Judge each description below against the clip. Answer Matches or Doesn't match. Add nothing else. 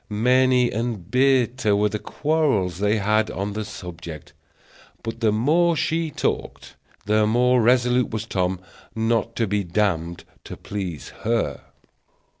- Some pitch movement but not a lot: Matches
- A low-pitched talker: Matches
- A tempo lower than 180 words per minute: Matches